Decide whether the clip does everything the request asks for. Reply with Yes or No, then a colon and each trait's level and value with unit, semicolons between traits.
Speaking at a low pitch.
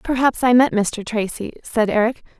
No: high, 230 Hz